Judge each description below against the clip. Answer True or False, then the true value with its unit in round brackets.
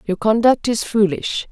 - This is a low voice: False (215 Hz)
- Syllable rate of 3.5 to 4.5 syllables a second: True (4.4 syllables/s)